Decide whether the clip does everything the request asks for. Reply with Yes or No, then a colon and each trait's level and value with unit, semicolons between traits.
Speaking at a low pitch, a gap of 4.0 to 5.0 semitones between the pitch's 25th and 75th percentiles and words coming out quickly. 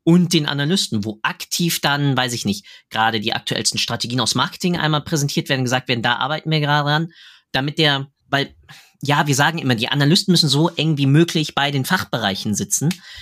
No: medium, 145 Hz; average, 4.3 semitones; fast, 195 wpm